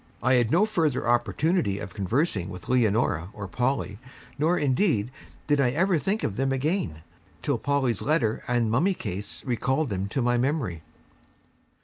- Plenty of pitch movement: Yes, wide, 6.1 semitones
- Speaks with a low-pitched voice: Yes, low, 125 Hz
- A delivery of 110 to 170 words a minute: Yes, average, 155 wpm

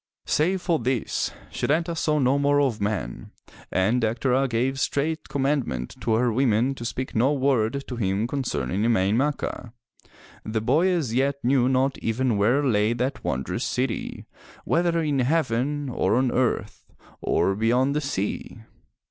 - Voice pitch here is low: Yes, low, 130 Hz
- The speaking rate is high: No, average, 150 wpm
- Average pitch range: Yes, average, 3.8 semitones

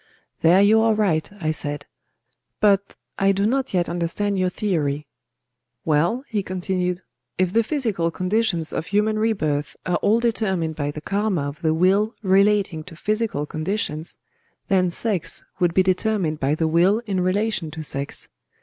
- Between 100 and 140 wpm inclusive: No, average, 160 wpm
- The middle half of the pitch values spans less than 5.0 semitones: Yes, average, 4.6 semitones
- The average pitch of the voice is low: No, medium, 185 Hz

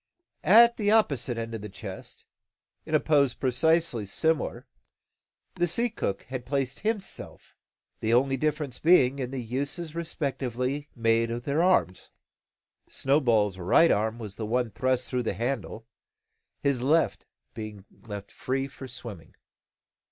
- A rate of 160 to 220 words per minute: No, average, 140 wpm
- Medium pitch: No, low, 130 Hz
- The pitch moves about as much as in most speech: Yes, average, 4.9 semitones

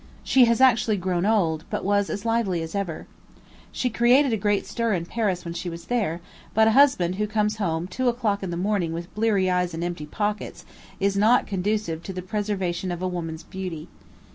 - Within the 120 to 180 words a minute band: No, fast, 205 wpm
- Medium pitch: No, high, 195 Hz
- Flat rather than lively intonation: No, average, 3.8 semitones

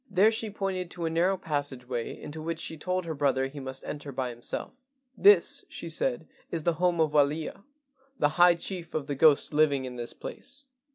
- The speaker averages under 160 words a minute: No, fast, 205 wpm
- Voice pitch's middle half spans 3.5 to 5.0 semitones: Yes, average, 4.3 semitones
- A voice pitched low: No, medium, 160 Hz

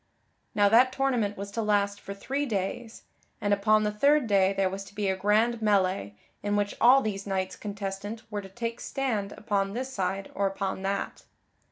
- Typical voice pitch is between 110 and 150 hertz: No, high, 205 Hz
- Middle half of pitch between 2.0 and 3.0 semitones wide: Yes, narrow, 2.5 semitones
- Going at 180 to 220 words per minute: Yes, average, 190 wpm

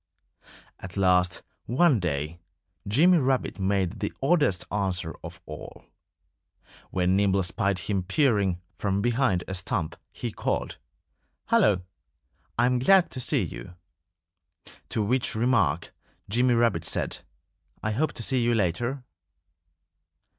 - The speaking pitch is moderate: No, low, 100 Hz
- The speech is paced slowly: Yes, slow, 120 wpm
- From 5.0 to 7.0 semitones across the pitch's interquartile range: Yes, wide, 5.5 semitones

